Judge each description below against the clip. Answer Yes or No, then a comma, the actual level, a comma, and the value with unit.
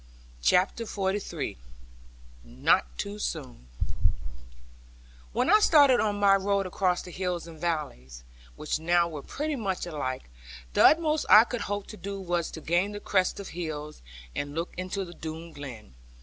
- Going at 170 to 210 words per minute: No, average, 155 wpm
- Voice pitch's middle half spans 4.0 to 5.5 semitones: Yes, average, 4.9 semitones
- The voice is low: No, medium, 175 Hz